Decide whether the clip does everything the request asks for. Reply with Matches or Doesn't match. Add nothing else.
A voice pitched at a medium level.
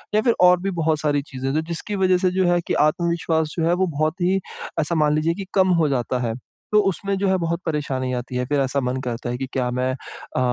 Matches